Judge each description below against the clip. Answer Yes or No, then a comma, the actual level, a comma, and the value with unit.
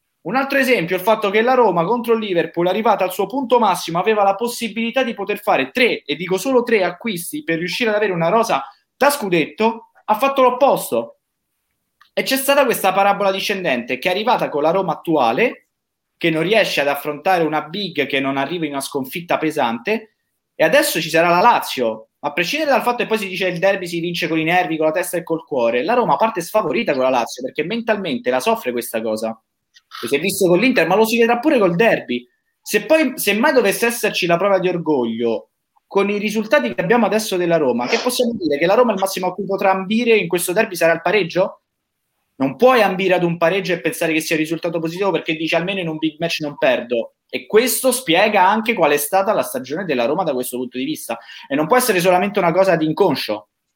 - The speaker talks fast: Yes, fast, 230 wpm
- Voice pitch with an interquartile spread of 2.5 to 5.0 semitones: No, wide, 5.4 semitones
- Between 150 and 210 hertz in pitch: Yes, high, 190 Hz